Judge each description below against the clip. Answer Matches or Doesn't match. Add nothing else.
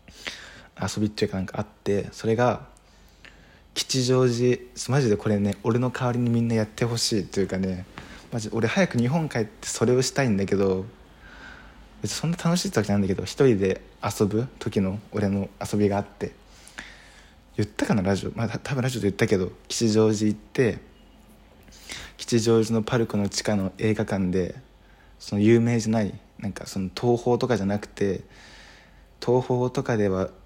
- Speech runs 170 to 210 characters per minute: Doesn't match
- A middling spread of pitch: Matches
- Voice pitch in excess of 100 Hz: Matches